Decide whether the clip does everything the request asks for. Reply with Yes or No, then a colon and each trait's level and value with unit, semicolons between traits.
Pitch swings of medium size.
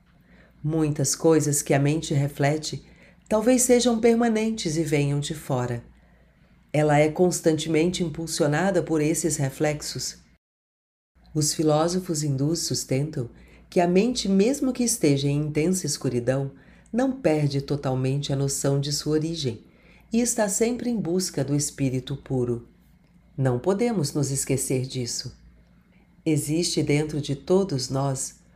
Yes: average, 4.2 semitones